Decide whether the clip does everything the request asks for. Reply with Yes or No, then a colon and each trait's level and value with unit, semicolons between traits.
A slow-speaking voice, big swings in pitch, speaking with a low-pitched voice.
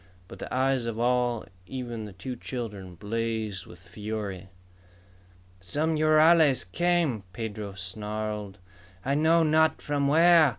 Yes: slow, 125 wpm; wide, 6.3 semitones; low, 115 Hz